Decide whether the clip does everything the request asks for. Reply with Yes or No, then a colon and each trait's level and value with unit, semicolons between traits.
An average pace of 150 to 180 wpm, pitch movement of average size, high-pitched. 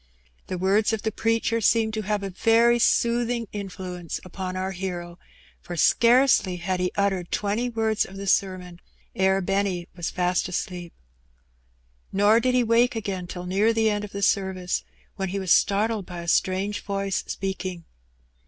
Yes: average, 170 wpm; average, 3.2 semitones; high, 195 Hz